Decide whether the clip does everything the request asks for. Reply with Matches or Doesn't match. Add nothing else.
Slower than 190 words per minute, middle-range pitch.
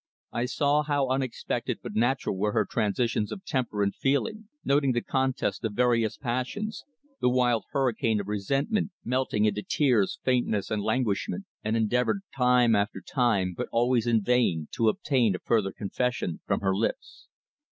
Doesn't match